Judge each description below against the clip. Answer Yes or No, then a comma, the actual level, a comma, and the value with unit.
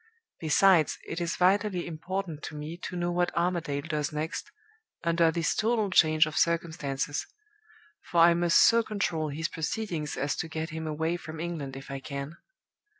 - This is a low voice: No, medium, 165 Hz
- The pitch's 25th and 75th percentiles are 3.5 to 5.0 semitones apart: No, narrow, 2.4 semitones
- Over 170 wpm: No, average, 165 wpm